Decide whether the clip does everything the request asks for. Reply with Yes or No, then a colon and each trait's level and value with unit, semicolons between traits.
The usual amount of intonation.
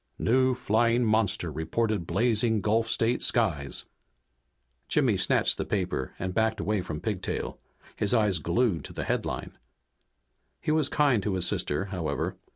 Yes: average, 4.3 semitones